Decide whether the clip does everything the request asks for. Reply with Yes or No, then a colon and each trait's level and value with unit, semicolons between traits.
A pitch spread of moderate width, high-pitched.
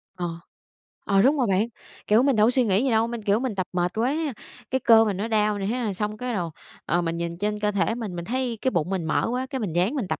Yes: average, 4.2 semitones; high, 210 Hz